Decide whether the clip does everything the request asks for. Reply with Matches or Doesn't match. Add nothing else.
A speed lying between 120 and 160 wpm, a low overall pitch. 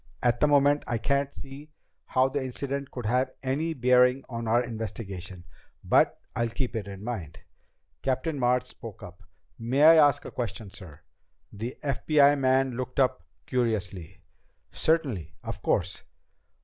Matches